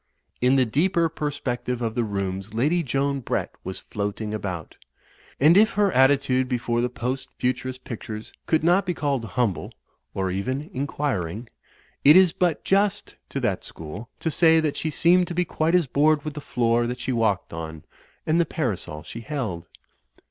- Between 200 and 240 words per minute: No, average, 175 wpm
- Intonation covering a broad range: Yes, wide, 6.0 semitones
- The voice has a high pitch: No, low, 130 Hz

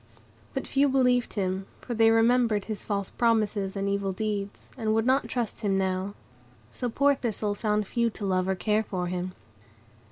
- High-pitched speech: Yes, high, 210 Hz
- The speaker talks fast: No, average, 180 wpm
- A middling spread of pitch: Yes, average, 3.2 semitones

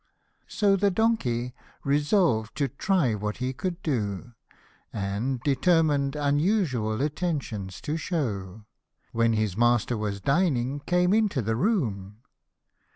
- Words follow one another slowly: Yes, slow, 115 wpm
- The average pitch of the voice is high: No, low, 135 Hz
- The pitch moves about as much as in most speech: No, wide, 7.5 semitones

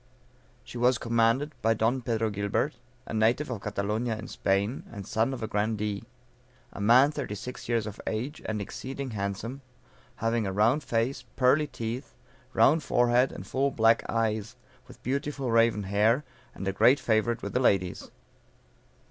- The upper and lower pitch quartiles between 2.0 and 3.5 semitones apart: Yes, average, 3.2 semitones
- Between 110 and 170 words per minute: Yes, average, 160 wpm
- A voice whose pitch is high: No, low, 115 Hz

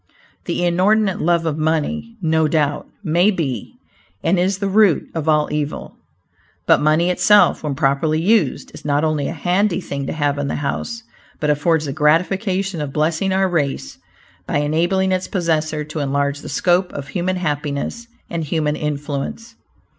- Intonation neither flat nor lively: Yes, average, 3.9 semitones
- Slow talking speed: No, average, 165 wpm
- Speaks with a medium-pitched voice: Yes, medium, 160 Hz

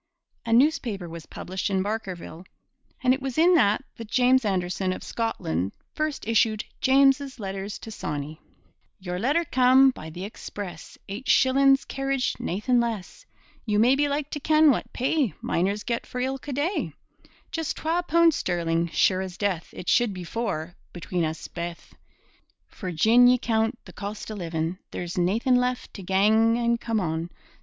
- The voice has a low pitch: No, high, 220 Hz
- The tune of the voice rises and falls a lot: Yes, wide, 6.3 semitones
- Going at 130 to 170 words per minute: Yes, average, 165 wpm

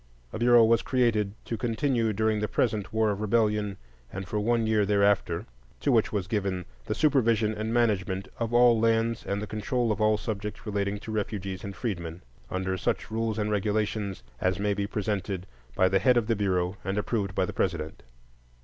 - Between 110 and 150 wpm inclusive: No, average, 195 wpm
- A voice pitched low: Yes, low, 105 Hz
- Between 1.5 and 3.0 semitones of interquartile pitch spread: Yes, narrow, 2.4 semitones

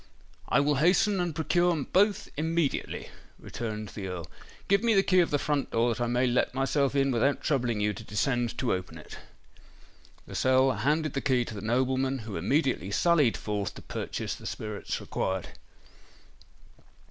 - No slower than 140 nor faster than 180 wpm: Yes, average, 170 wpm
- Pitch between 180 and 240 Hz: No, low, 130 Hz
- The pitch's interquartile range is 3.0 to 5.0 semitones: No, wide, 5.4 semitones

